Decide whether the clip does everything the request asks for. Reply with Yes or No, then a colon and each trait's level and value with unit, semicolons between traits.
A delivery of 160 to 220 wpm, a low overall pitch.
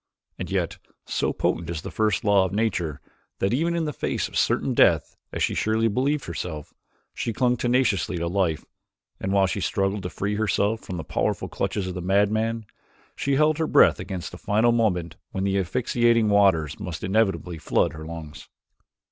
Yes: average, 185 wpm; low, 100 Hz